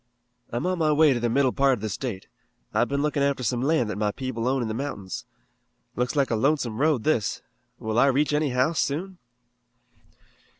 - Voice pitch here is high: No, low, 130 Hz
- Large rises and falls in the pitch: No, average, 4.1 semitones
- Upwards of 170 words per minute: Yes, fast, 205 wpm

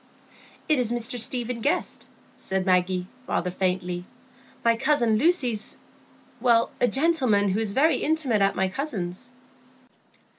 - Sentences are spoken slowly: Yes, slow, 115 wpm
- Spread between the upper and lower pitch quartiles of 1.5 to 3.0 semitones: No, average, 5.3 semitones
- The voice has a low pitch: No, high, 230 Hz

